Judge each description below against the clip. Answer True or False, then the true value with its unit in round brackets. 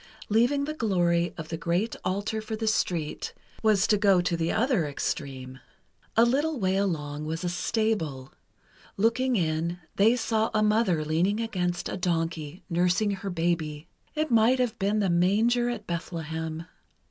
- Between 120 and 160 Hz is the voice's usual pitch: False (190 Hz)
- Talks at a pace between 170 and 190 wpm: False (160 wpm)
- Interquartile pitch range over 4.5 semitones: True (5.1 semitones)